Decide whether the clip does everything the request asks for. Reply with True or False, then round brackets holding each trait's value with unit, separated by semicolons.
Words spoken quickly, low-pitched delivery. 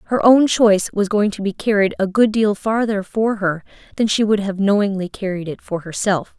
False (215 wpm; 205 Hz)